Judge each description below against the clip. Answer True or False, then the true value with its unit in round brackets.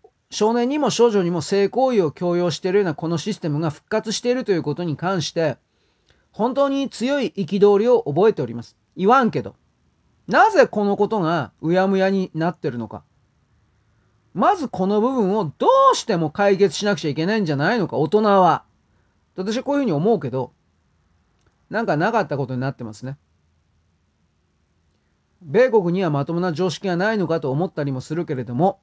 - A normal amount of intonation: False (8.7 semitones)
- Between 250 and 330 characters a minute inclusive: False (355 characters per minute)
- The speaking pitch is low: False (175 Hz)